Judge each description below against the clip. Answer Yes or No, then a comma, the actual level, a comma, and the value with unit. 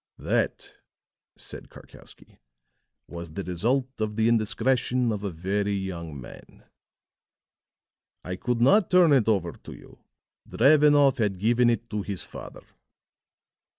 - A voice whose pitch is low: Yes, low, 110 Hz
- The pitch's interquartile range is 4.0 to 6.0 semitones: Yes, average, 4.7 semitones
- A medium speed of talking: No, slow, 125 wpm